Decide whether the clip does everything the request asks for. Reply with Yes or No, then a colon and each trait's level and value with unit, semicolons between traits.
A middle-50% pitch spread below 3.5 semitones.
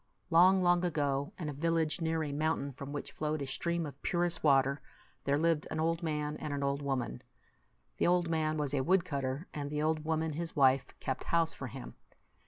Yes: average, 2.9 semitones